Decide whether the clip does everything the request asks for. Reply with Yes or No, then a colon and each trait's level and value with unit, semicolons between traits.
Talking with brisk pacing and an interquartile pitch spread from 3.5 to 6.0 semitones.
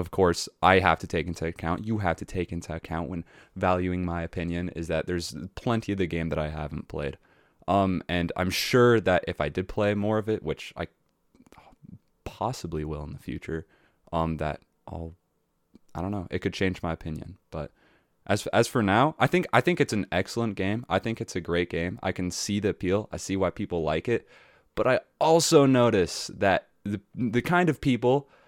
Yes: fast, 210 wpm; average, 4.2 semitones